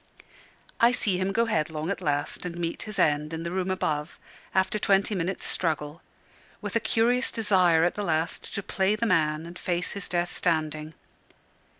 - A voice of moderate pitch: Yes, medium, 180 Hz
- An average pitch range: Yes, average, 3.9 semitones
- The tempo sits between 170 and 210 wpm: Yes, average, 180 wpm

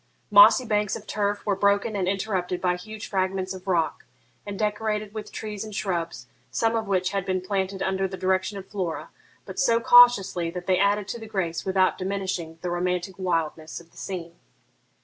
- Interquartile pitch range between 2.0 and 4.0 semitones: Yes, narrow, 2.4 semitones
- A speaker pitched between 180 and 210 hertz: Yes, high, 190 Hz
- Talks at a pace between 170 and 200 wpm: Yes, average, 190 wpm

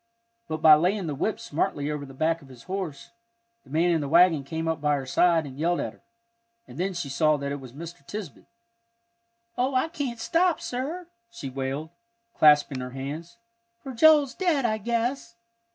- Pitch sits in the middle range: Yes, medium, 165 Hz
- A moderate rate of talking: Yes, average, 190 wpm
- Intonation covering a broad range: Yes, wide, 8.3 semitones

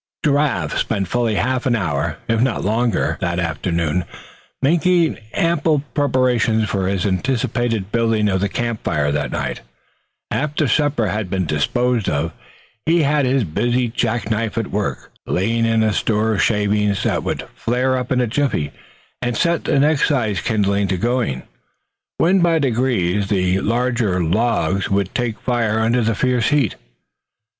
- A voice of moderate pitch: No, low, 115 Hz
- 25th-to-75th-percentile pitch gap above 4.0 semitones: Yes, average, 4.4 semitones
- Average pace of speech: Yes, average, 155 wpm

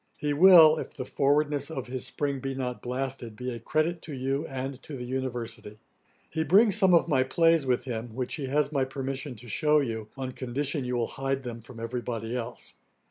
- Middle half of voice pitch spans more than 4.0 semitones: No, average, 3.2 semitones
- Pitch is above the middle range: No, low, 130 Hz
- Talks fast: Yes, fast, 210 wpm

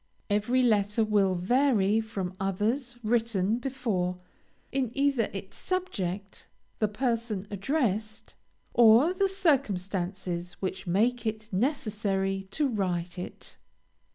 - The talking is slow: Yes, slow, 105 wpm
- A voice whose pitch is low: No, high, 215 Hz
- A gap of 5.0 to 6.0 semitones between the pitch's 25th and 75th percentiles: No, average, 4.2 semitones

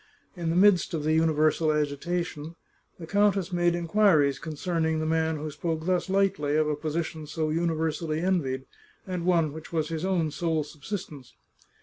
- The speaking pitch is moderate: Yes, medium, 160 Hz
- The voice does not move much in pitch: Yes, narrow, 2.1 semitones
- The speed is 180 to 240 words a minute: No, average, 160 wpm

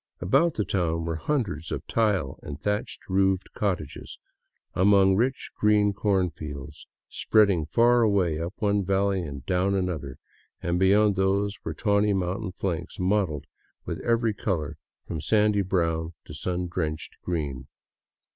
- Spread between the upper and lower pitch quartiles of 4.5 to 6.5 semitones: No, average, 3.7 semitones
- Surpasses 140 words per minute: No, slow, 135 wpm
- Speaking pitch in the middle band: No, very low, 95 Hz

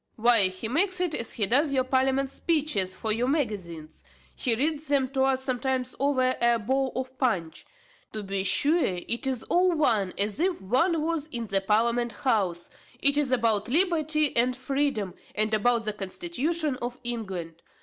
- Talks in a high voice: Yes, very high, 250 Hz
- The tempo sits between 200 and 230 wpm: No, average, 170 wpm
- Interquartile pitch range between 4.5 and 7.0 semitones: Yes, average, 5.0 semitones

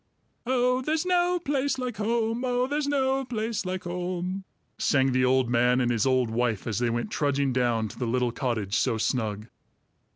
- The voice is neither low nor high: Yes, medium, 150 Hz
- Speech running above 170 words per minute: Yes, average, 185 wpm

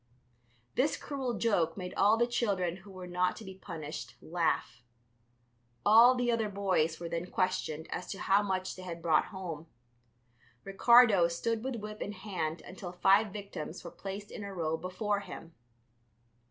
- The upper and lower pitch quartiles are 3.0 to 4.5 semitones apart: Yes, average, 3.6 semitones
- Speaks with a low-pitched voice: No, high, 190 Hz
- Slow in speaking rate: No, average, 165 wpm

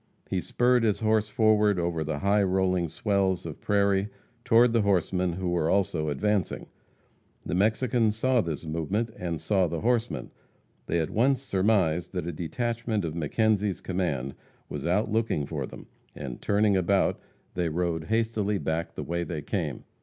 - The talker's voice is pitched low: Yes, very low, 95 Hz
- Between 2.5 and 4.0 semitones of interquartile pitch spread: No, average, 4.4 semitones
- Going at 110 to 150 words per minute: No, average, 160 wpm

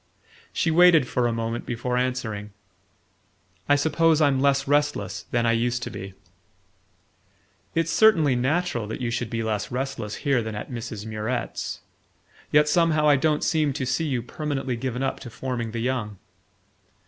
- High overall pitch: No, low, 125 Hz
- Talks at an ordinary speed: Yes, average, 160 wpm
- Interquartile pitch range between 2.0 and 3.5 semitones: No, average, 4.3 semitones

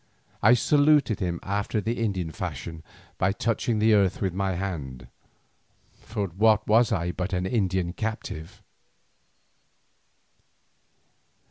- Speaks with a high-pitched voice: No, low, 100 Hz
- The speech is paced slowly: Yes, slow, 115 wpm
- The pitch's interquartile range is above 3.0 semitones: Yes, average, 3.7 semitones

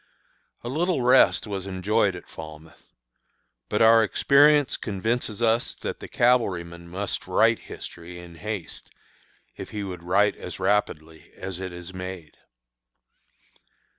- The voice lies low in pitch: Yes, very low, 95 Hz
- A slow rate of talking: Yes, slow, 130 wpm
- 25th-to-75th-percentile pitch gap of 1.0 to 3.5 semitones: No, average, 4.6 semitones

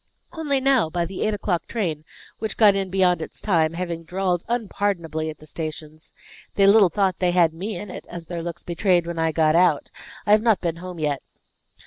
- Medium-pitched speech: Yes, medium, 175 Hz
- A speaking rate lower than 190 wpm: No, fast, 205 wpm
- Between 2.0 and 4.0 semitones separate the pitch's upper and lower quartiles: Yes, average, 3.6 semitones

